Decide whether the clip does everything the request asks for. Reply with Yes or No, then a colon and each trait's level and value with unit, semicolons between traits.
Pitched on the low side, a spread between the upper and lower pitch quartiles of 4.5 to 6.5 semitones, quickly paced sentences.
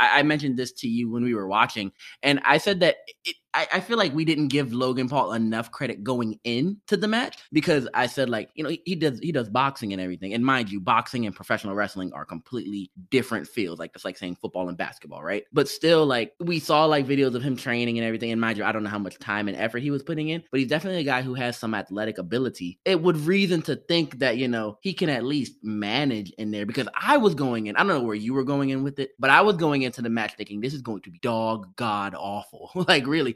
Yes: low, 125 Hz; wide, 5.6 semitones; fast, 265 wpm